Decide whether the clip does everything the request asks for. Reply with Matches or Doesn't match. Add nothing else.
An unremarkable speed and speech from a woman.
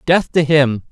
Doesn't match